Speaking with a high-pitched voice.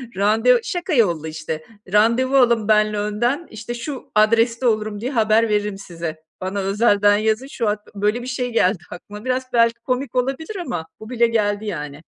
Yes: high, 220 Hz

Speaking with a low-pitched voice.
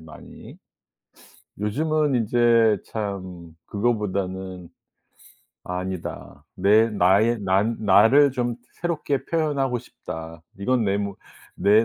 Yes: low, 105 Hz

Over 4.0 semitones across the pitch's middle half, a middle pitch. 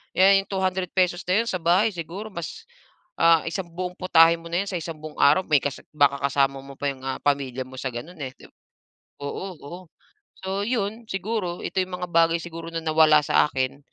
Yes: average, 4.6 semitones; medium, 170 Hz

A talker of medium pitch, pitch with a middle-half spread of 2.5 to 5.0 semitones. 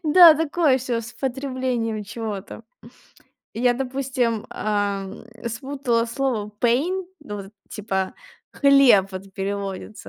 No: high, 235 Hz; average, 4.6 semitones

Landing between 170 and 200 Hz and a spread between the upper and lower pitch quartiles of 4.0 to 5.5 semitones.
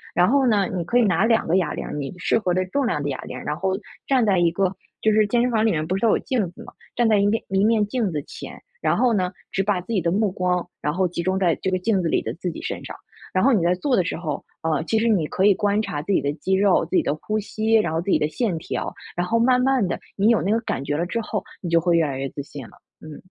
Yes: high, 190 Hz; average, 4.4 semitones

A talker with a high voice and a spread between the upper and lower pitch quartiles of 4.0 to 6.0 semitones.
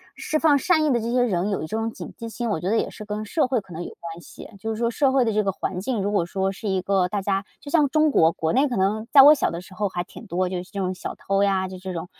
Yes: high, 205 Hz; average, 4.3 semitones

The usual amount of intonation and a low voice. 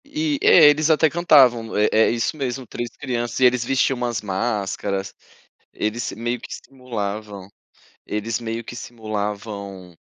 Yes: average, 3.6 semitones; low, 115 Hz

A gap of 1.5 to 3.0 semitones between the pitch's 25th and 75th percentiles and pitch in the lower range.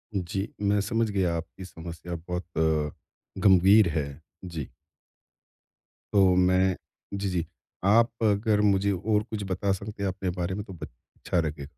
Yes: average, 2.7 semitones; very low, 95 Hz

